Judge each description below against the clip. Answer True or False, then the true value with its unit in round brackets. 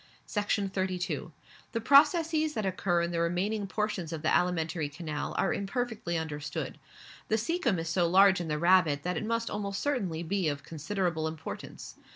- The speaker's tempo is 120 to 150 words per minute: False (170 wpm)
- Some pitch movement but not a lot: True (4.5 semitones)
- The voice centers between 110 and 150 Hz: False (180 Hz)